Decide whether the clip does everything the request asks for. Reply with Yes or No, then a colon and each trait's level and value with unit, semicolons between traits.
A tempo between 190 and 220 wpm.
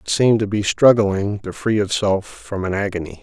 Yes: fast, 205 wpm